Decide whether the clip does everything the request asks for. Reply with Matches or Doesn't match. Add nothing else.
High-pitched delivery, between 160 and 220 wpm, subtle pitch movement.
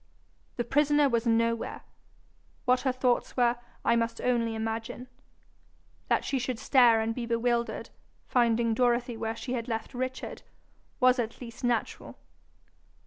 Doesn't match